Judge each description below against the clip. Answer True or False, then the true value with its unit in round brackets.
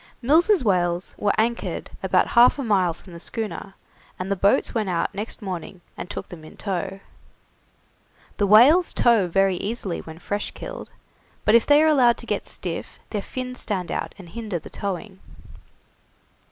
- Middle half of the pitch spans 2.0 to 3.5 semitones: False (4.4 semitones)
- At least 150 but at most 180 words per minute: True (170 wpm)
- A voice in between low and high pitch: False (205 Hz)